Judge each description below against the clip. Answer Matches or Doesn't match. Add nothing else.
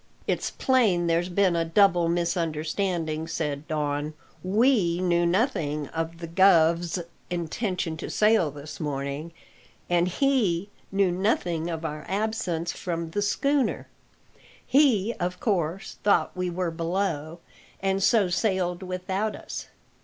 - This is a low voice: Doesn't match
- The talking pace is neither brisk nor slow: Doesn't match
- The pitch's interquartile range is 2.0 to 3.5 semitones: Matches